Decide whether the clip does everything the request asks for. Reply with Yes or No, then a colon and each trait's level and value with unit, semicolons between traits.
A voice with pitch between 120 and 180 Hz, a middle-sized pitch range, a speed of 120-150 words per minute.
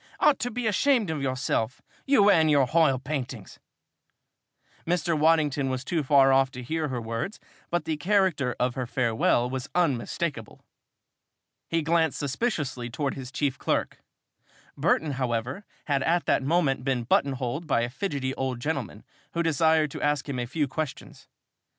No: medium, 140 Hz; average, 4.1 semitones; average, 160 wpm